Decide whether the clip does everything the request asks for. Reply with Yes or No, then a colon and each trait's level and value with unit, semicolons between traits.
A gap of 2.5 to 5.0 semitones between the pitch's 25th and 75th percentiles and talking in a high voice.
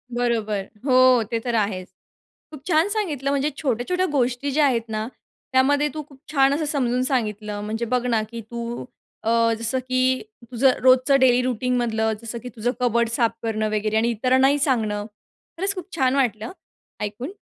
Yes: average, 3.2 semitones; high, 245 Hz